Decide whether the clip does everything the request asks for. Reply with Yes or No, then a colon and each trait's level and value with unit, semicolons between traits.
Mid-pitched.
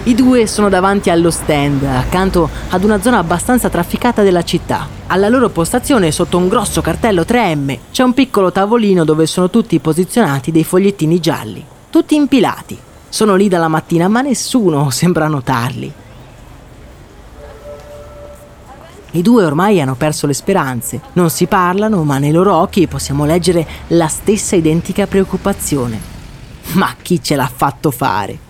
Yes: medium, 175 Hz